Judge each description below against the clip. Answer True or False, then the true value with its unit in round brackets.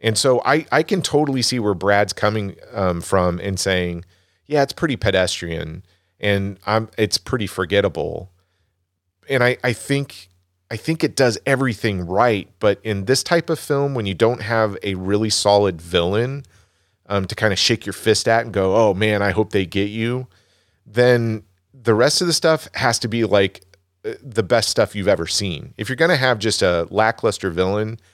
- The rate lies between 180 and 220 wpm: True (190 wpm)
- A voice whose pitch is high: False (105 Hz)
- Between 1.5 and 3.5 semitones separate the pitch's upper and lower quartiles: False (4.5 semitones)